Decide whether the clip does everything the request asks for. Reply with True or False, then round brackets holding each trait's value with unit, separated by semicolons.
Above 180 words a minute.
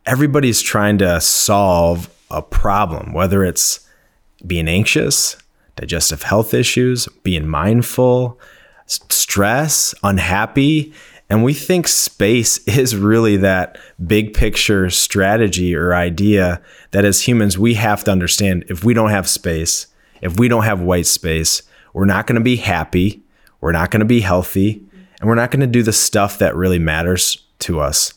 False (155 wpm)